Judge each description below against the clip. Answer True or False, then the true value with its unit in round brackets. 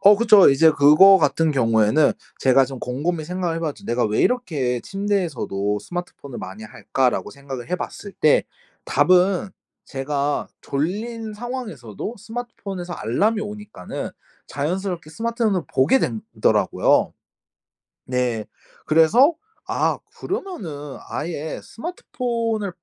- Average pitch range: False (7.6 semitones)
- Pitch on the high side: False (165 Hz)